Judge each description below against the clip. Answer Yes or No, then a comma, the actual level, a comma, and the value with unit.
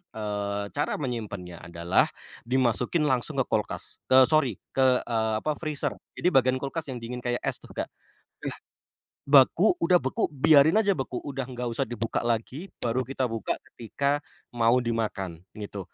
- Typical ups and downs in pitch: Yes, average, 3.6 semitones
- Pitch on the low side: Yes, low, 125 Hz